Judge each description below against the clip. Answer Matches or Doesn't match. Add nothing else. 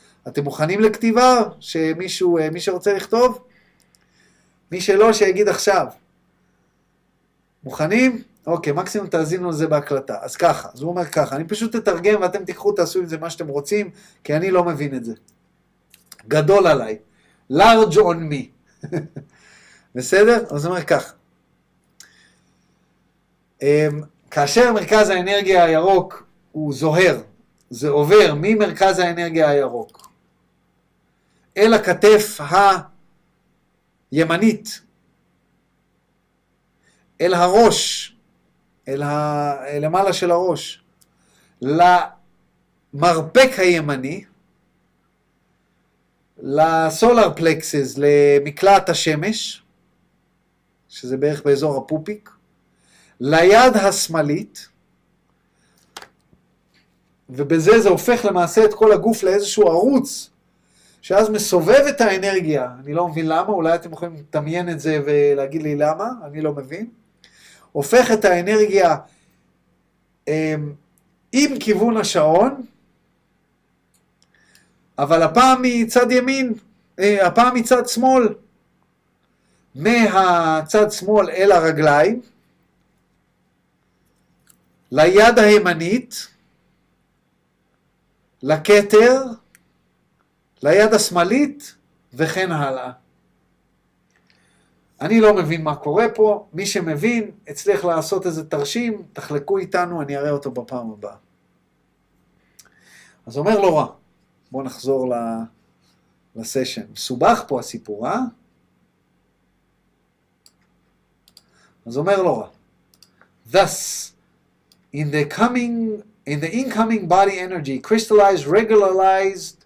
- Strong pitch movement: Matches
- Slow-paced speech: Matches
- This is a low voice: Doesn't match